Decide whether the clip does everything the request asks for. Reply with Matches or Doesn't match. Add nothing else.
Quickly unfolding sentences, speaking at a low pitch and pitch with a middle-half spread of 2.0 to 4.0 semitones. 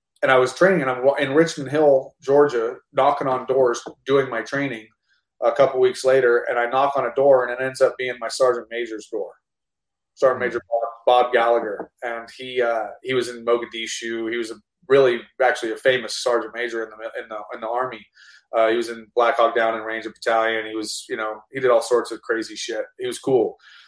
Matches